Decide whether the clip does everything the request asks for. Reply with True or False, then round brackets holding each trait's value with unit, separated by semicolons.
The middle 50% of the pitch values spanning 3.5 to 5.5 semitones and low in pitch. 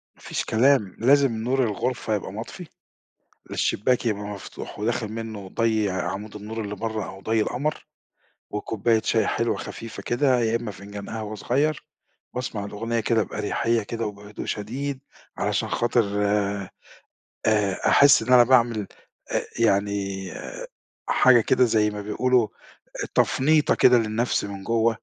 False (2.7 semitones; 110 Hz)